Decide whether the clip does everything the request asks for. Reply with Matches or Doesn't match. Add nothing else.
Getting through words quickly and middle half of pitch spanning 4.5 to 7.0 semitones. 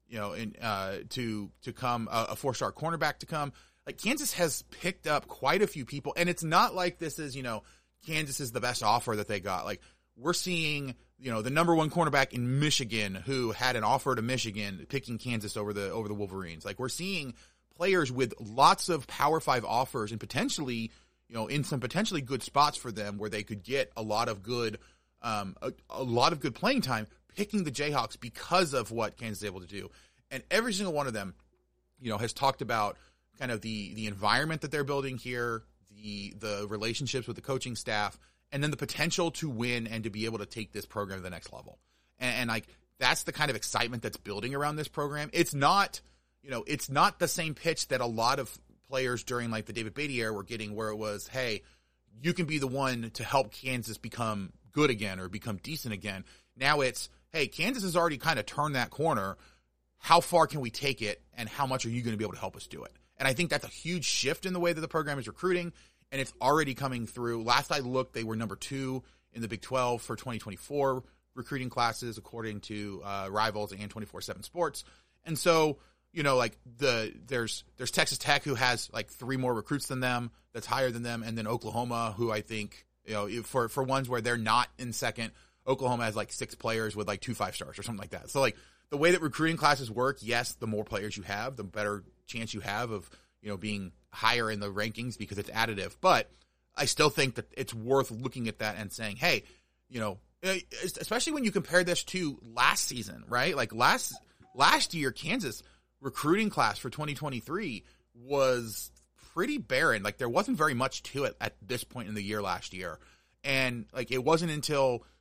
Matches